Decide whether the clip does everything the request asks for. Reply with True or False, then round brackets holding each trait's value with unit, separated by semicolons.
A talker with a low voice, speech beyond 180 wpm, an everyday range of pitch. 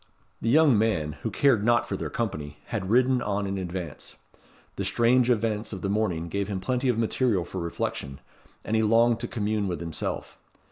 True (105 Hz; 190 wpm; 4.0 semitones)